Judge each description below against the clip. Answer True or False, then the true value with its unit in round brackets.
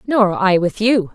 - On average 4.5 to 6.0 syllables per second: False (4.0 syllables/s)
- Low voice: False (205 Hz)